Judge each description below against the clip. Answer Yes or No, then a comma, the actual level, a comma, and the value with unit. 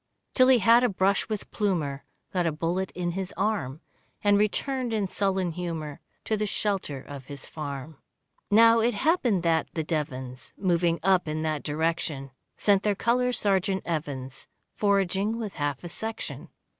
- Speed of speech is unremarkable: Yes, average, 160 wpm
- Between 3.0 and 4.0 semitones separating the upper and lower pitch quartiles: No, average, 5.2 semitones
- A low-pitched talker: No, medium, 185 Hz